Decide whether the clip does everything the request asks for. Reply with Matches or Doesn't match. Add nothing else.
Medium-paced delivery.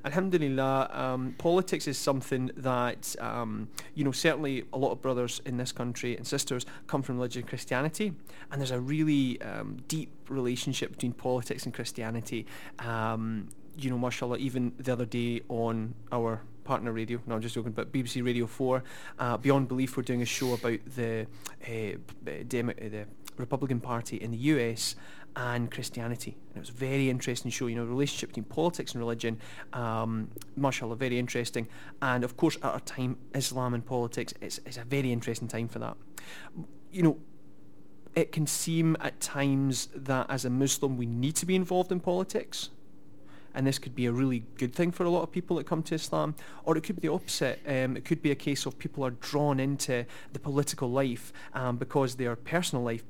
Matches